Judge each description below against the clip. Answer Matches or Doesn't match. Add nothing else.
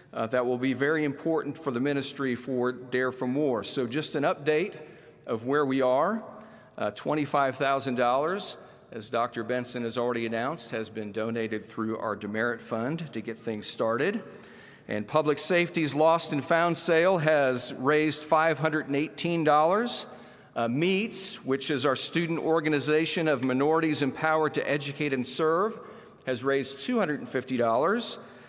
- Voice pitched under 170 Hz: Matches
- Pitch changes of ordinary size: Matches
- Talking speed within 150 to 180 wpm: Doesn't match